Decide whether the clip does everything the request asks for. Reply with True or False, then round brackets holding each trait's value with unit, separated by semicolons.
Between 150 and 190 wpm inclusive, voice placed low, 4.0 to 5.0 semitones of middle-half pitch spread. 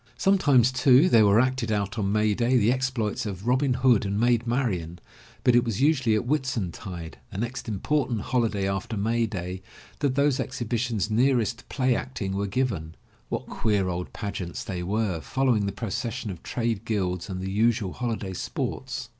True (180 wpm; 115 Hz; 4.4 semitones)